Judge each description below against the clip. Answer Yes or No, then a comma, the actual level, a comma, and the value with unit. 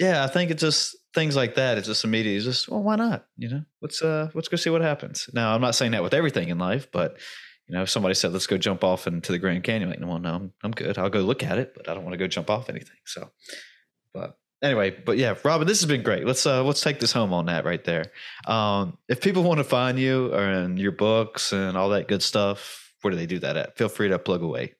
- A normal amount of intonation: No, wide, 7.9 semitones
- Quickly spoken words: Yes, fast, 280 wpm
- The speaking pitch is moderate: No, low, 120 Hz